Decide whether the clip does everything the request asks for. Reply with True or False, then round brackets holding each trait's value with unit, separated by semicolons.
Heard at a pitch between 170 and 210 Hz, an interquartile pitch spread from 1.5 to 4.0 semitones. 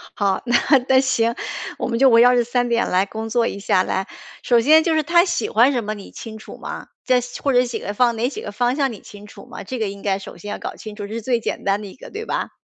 False (230 Hz; 3.5 semitones)